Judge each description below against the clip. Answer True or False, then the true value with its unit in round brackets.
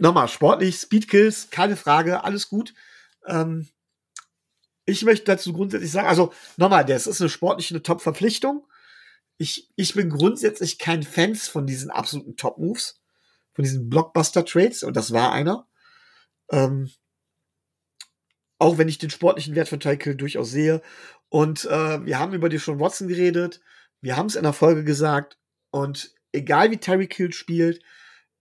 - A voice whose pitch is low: False (165 Hz)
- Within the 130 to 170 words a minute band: True (150 wpm)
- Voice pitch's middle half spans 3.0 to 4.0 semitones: False (4.5 semitones)